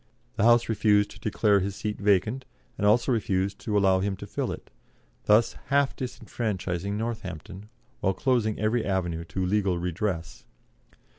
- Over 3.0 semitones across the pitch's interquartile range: No, average, 2.7 semitones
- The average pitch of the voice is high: No, low, 105 Hz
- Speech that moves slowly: No, average, 150 wpm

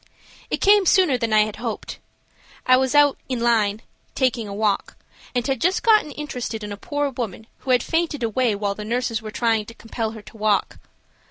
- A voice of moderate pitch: No, high, 235 Hz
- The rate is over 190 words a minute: Yes, average, 200 wpm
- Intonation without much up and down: No, average, 3.7 semitones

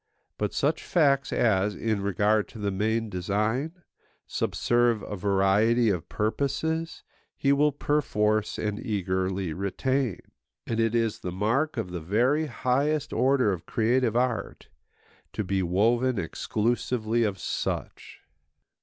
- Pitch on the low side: Yes, low, 110 Hz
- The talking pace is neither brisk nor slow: No, slow, 125 wpm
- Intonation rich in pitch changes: No, average, 4.4 semitones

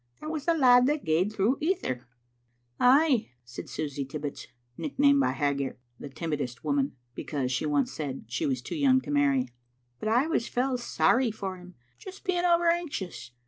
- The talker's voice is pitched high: Yes, high, 210 Hz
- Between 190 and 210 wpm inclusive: No, average, 180 wpm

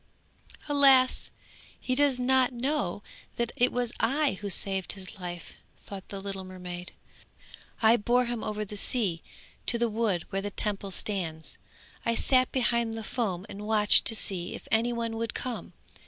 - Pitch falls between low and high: No, high, 220 Hz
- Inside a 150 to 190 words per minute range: Yes, average, 165 wpm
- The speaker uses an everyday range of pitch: Yes, average, 4.0 semitones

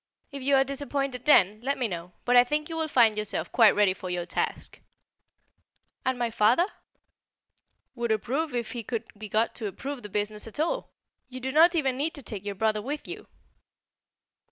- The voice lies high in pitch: Yes, high, 245 Hz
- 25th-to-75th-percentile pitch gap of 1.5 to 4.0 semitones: No, average, 4.8 semitones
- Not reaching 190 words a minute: No, average, 195 wpm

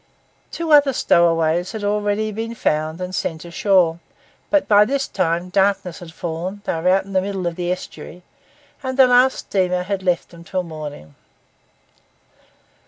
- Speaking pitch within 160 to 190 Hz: Yes, medium, 185 Hz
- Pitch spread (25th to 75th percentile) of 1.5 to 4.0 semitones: Yes, average, 3.4 semitones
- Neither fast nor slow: Yes, average, 170 wpm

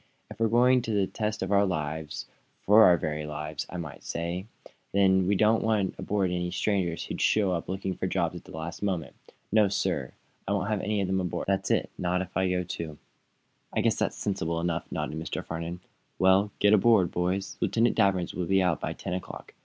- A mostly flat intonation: No, average, 3.0 semitones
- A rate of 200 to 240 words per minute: Yes, fast, 205 wpm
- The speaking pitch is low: Yes, very low, 95 Hz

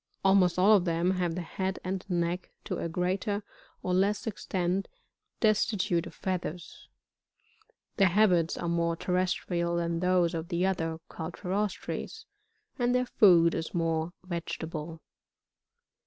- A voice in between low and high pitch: Yes, medium, 180 Hz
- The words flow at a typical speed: No, slow, 130 wpm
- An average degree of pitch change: No, narrow, 2.2 semitones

